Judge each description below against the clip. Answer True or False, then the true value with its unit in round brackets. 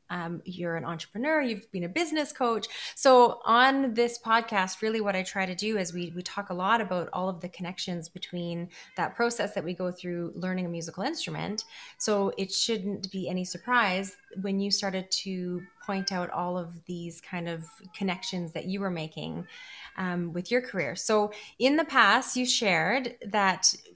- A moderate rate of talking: True (185 wpm)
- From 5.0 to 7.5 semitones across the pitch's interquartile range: False (3.8 semitones)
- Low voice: False (190 Hz)